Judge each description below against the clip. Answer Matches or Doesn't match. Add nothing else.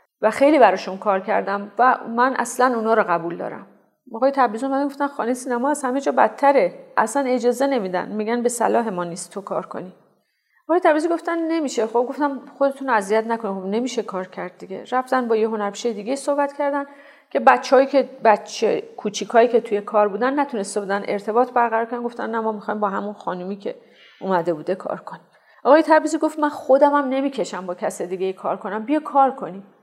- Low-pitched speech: Doesn't match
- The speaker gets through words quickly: Matches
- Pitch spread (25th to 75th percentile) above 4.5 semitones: Matches